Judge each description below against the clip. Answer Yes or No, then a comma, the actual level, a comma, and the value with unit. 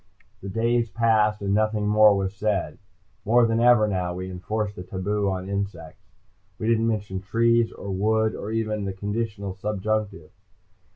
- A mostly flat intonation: Yes, narrow, 2.3 semitones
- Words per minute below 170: Yes, average, 160 wpm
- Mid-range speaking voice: No, low, 105 Hz